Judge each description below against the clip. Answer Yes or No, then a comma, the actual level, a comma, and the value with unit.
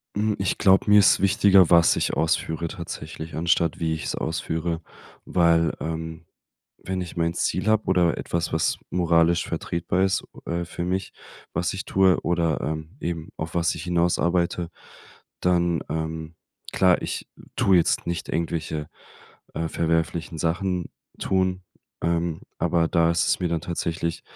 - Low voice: Yes, very low, 85 Hz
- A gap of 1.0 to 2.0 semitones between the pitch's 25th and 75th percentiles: Yes, narrow, 1.6 semitones